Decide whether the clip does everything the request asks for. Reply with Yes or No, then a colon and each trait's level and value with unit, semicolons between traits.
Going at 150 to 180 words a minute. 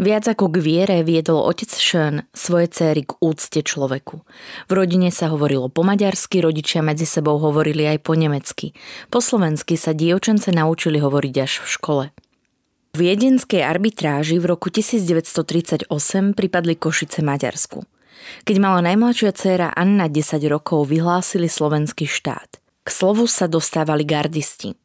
No: average, 140 wpm